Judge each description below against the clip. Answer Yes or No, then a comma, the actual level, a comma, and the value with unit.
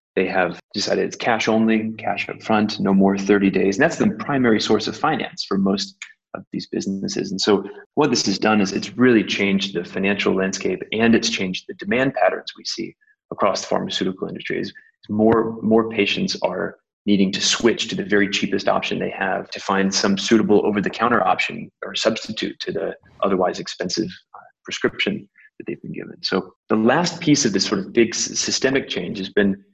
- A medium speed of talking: Yes, average, 195 wpm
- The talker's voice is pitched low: Yes, low, 105 Hz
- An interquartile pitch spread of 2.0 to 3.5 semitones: Yes, narrow, 2.4 semitones